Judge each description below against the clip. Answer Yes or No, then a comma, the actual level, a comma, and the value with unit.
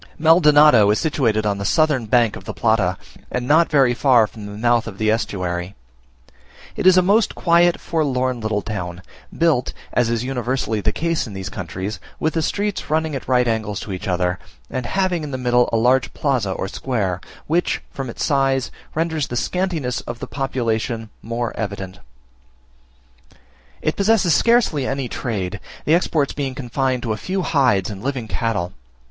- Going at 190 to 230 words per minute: No, average, 175 wpm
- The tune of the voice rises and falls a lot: Yes, wide, 5.9 semitones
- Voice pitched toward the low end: Yes, low, 125 Hz